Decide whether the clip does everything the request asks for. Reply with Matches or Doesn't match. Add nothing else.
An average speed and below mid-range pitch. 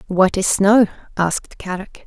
Doesn't match